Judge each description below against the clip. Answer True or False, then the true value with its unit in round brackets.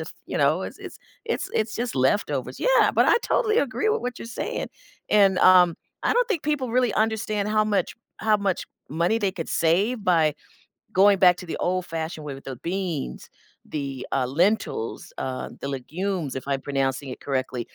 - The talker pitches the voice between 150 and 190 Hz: True (185 Hz)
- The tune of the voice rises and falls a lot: True (7.3 semitones)